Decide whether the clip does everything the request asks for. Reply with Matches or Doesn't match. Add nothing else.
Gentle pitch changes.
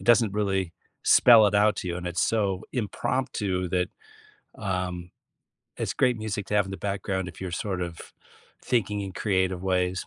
Matches